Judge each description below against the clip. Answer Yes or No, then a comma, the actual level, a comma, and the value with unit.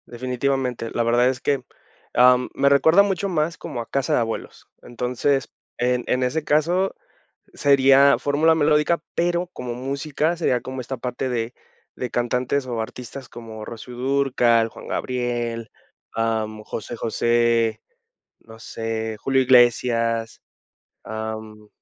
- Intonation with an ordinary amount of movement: Yes, average, 3.1 semitones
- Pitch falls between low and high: No, low, 125 Hz